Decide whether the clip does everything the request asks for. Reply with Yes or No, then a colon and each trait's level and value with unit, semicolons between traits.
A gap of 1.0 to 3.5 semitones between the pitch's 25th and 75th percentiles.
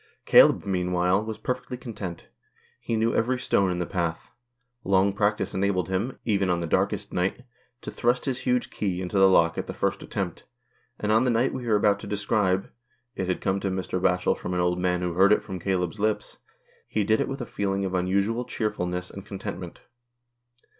Yes: average, 3.2 semitones